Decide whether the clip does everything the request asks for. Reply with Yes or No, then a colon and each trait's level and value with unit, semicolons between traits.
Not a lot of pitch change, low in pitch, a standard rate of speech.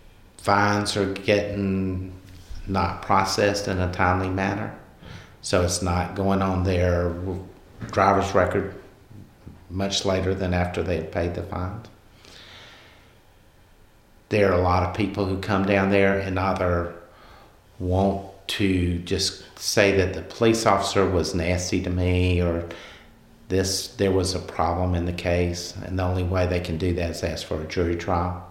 Yes: narrow, 1.7 semitones; very low, 95 Hz; average, 155 wpm